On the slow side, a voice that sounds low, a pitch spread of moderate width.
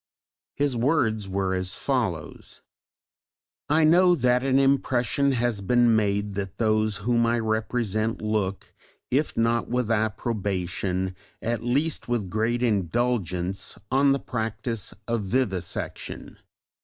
Yes: slow, 120 wpm; low, 115 Hz; average, 3.7 semitones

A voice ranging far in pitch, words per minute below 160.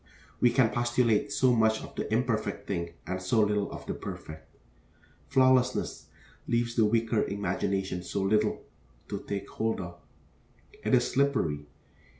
No: average, 3.7 semitones; average, 145 wpm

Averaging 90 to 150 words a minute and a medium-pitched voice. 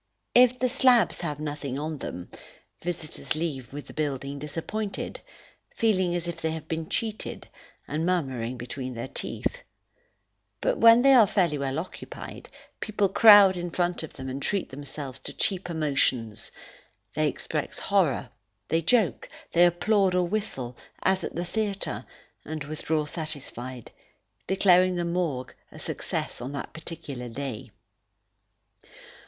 Yes: average, 140 wpm; medium, 160 Hz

